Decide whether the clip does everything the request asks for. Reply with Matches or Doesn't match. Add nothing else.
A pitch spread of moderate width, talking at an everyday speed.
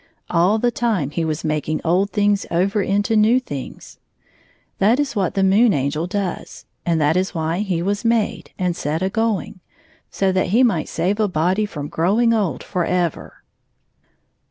Matches